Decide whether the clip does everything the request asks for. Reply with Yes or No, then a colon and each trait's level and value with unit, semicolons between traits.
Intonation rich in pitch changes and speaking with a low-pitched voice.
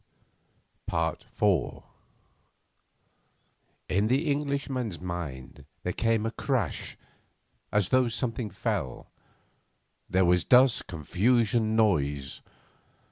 Yes: wide, 5.9 semitones; low, 110 Hz